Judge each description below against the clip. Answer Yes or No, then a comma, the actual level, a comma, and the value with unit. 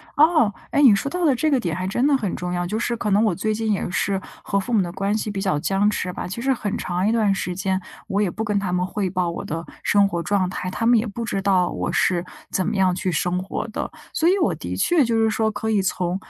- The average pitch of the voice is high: Yes, high, 200 Hz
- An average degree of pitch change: Yes, average, 3.4 semitones